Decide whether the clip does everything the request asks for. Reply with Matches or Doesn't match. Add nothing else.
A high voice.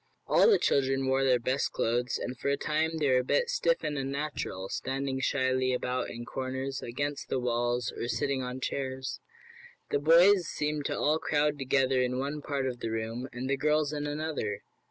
Doesn't match